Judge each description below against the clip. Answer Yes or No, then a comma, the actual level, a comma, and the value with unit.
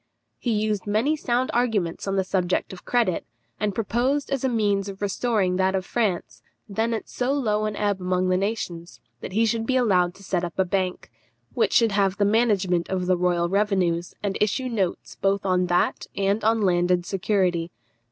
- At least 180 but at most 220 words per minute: Yes, average, 190 wpm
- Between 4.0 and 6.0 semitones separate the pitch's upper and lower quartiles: No, average, 3.4 semitones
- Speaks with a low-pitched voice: No, high, 200 Hz